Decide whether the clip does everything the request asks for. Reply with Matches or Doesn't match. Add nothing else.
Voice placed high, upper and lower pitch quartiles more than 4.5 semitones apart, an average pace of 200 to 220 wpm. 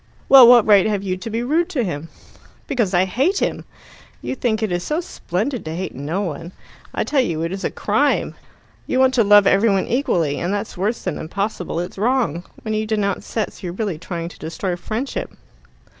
Matches